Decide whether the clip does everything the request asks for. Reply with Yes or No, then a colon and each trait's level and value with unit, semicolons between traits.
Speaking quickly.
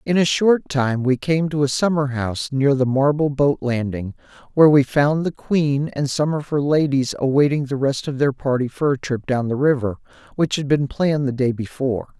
Yes: fast, 215 wpm